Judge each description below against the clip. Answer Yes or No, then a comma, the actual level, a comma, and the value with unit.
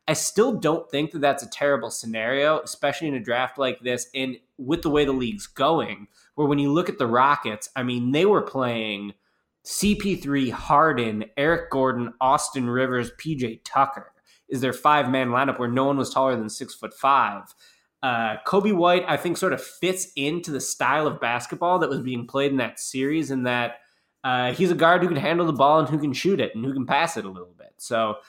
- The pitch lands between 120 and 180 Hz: Yes, low, 135 Hz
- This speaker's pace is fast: Yes, fast, 215 wpm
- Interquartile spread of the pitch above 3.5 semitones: Yes, average, 3.9 semitones